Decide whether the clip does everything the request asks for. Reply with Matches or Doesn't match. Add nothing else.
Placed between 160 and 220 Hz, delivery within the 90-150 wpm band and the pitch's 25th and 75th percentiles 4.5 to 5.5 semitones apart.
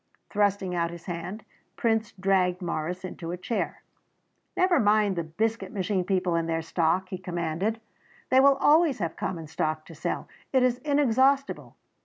Doesn't match